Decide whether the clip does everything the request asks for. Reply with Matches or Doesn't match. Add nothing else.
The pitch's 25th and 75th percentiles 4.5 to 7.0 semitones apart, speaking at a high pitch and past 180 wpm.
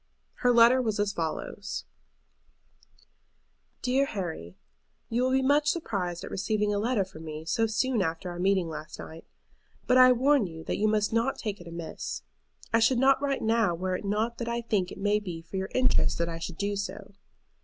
Matches